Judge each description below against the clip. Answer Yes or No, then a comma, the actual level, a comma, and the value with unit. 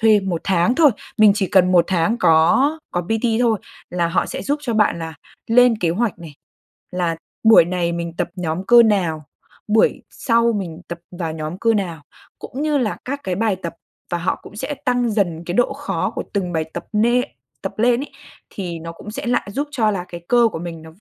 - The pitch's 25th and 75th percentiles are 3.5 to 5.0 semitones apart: No, wide, 5.5 semitones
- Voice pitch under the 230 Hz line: Yes, high, 195 Hz